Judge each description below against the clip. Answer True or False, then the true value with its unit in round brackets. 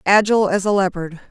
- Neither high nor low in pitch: False (195 Hz)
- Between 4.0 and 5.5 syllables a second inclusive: False (6.3 syllables/s)